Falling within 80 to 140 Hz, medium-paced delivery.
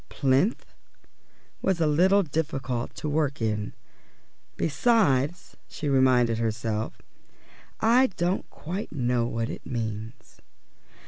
No: low, 135 Hz; slow, 105 wpm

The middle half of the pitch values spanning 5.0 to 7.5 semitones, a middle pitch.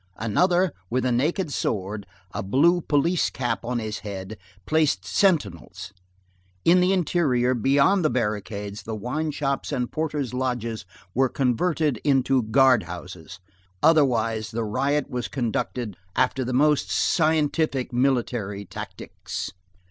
No: wide, 5.4 semitones; low, 130 Hz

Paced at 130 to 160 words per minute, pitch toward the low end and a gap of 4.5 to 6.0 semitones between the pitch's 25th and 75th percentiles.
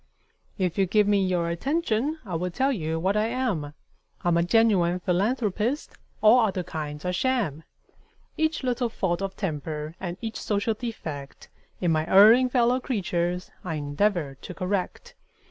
No: average, 155 wpm; high, 190 Hz; average, 5.1 semitones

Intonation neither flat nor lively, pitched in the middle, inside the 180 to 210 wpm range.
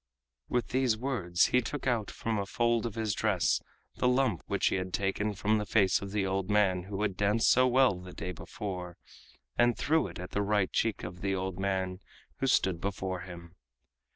No: average, 3.6 semitones; low, 100 Hz; fast, 205 wpm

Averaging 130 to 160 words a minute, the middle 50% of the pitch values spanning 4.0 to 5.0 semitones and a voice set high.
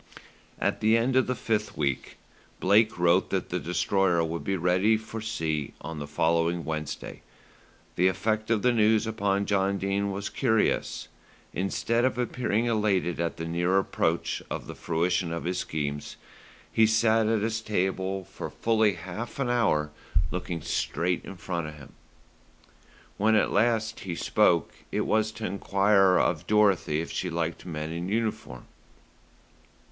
No: average, 155 wpm; average, 4.5 semitones; very low, 95 Hz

